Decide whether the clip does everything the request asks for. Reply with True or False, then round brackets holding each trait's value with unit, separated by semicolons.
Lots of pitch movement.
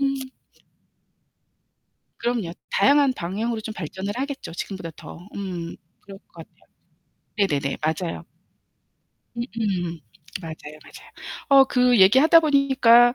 True (6.5 semitones)